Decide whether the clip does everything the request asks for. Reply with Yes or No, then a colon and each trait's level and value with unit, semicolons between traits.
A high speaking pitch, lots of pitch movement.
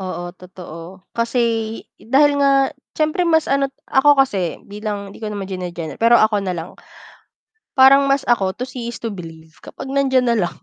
Yes: high, 225 Hz; wide, 6.7 semitones